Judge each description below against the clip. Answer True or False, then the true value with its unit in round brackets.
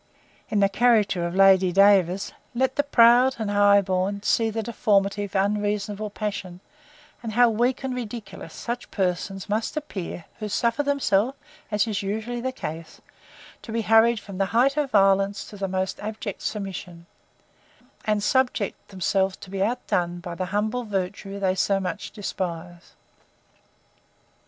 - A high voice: True (205 Hz)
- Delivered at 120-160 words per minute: True (155 wpm)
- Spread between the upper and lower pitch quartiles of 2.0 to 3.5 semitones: True (3.1 semitones)